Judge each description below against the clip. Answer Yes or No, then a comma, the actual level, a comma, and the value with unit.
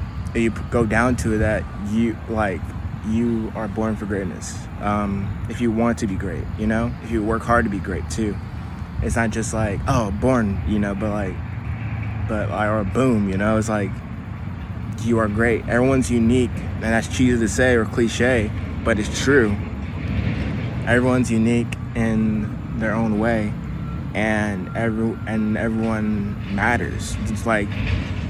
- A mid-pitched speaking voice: No, low, 110 Hz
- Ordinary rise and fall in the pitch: No, narrow, 2.1 semitones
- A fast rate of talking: No, average, 165 wpm